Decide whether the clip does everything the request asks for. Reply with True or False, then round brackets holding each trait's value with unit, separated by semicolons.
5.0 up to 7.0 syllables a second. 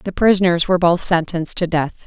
True (5.9 syllables/s)